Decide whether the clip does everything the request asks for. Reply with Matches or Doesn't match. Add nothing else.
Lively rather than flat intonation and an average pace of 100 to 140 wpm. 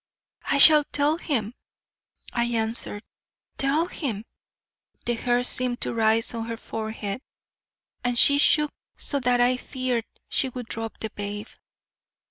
Doesn't match